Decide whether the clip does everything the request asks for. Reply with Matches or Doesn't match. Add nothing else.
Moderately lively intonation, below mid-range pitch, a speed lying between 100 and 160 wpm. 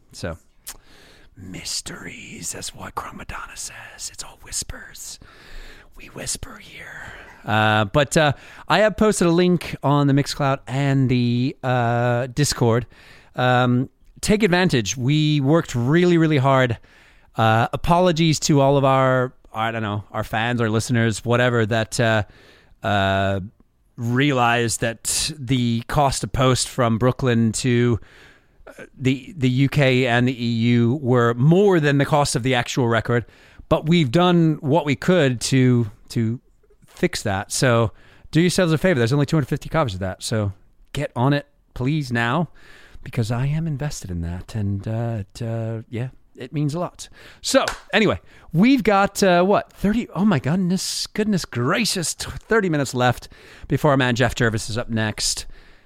Matches